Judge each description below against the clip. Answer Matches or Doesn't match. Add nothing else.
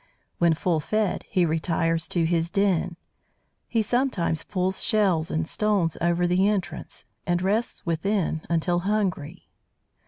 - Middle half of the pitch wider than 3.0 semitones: Matches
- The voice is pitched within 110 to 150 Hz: Doesn't match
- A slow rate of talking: Matches